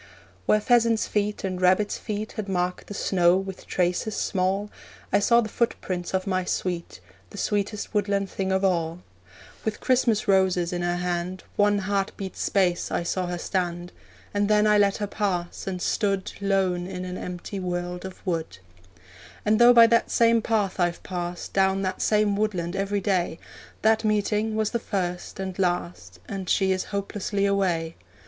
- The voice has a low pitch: No, high, 195 Hz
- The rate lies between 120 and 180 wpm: Yes, average, 170 wpm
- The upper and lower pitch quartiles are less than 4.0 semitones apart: Yes, narrow, 2.6 semitones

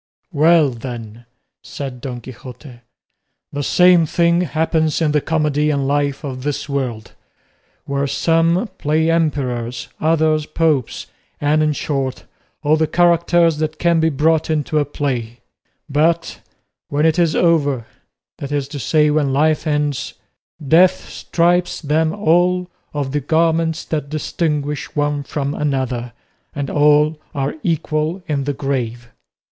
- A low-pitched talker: No, medium, 150 Hz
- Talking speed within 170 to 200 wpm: No, average, 140 wpm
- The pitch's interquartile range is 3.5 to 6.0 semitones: No, average, 2.7 semitones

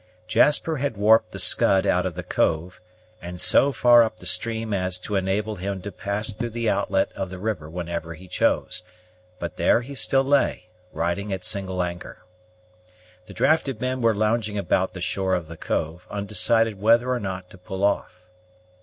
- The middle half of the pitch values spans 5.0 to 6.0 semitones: No, average, 3.7 semitones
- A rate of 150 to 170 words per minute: No, average, 180 wpm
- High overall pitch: No, low, 100 Hz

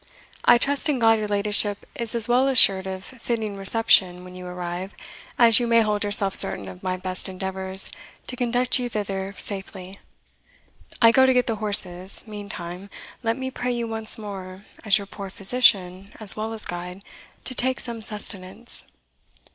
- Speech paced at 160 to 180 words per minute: Yes, average, 170 wpm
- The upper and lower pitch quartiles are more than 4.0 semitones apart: No, average, 3.5 semitones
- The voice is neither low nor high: No, high, 205 Hz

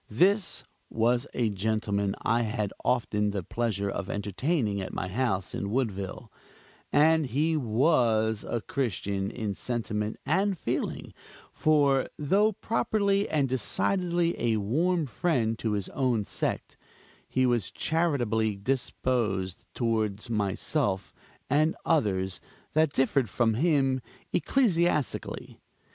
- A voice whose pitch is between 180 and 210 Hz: No, low, 120 Hz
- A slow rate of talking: Yes, slow, 115 wpm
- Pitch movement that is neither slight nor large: No, wide, 6.5 semitones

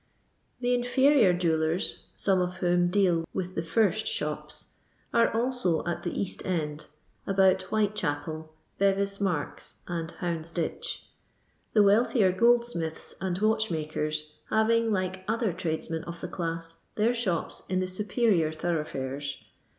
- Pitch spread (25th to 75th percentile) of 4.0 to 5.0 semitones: Yes, average, 4.6 semitones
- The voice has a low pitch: No, medium, 185 Hz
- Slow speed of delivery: Yes, slow, 125 wpm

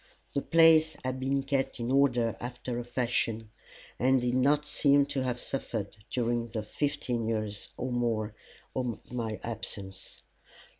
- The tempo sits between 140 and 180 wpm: Yes, average, 145 wpm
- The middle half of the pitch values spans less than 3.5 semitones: Yes, average, 2.9 semitones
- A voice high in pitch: No, low, 125 Hz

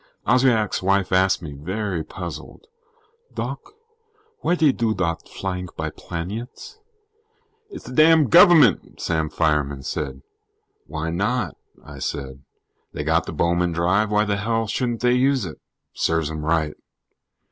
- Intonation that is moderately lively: No, wide, 6.6 semitones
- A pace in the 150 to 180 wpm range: No, slow, 135 wpm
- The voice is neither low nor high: No, very low, 95 Hz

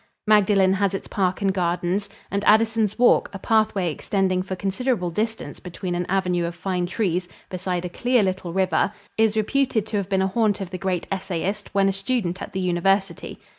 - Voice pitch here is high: Yes, high, 195 Hz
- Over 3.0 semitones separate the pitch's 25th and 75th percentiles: No, narrow, 2.6 semitones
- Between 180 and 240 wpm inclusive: Yes, average, 190 wpm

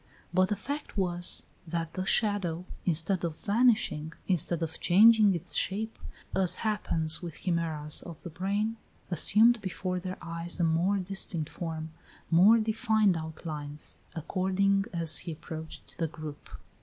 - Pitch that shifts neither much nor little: Yes, average, 3.6 semitones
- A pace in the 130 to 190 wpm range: Yes, average, 140 wpm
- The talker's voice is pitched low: No, medium, 175 Hz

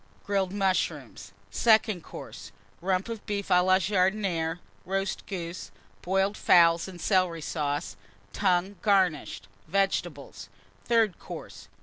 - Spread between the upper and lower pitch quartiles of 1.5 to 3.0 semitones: Yes, average, 2.7 semitones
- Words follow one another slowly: Yes, slow, 110 wpm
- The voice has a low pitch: No, medium, 185 Hz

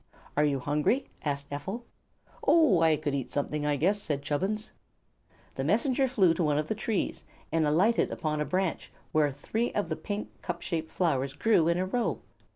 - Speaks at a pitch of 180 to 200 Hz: No, medium, 165 Hz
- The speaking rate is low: No, average, 185 wpm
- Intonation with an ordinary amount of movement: No, wide, 5.9 semitones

